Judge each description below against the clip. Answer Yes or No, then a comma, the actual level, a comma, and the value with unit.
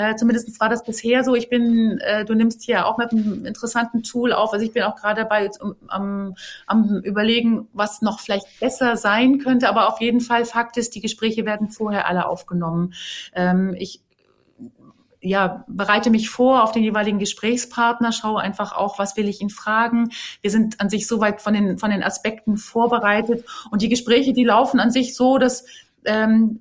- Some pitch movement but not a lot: No, narrow, 2.2 semitones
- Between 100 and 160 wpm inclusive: No, fast, 190 wpm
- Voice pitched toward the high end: Yes, high, 220 Hz